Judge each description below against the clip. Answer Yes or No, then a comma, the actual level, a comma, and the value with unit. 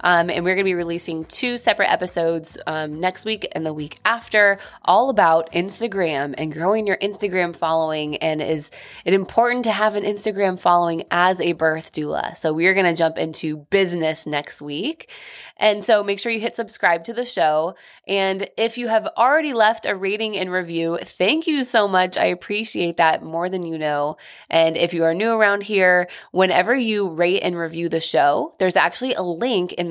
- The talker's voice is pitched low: No, medium, 185 Hz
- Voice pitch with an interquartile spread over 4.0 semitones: Yes, average, 4.6 semitones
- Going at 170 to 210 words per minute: Yes, average, 195 wpm